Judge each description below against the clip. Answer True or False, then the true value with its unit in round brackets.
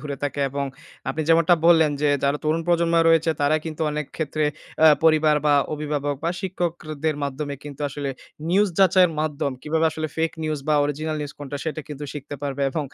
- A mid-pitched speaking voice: True (155 Hz)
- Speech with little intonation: True (2.0 semitones)